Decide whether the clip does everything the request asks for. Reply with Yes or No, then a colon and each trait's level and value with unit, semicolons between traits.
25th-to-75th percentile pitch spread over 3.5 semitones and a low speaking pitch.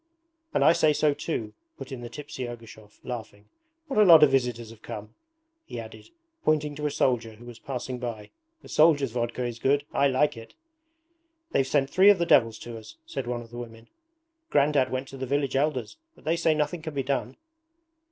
Yes: average, 4.0 semitones; low, 130 Hz